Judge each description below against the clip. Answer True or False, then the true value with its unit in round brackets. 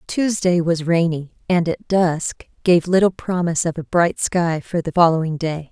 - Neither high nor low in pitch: True (170 Hz)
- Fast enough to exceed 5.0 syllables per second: False (4.5 syllables/s)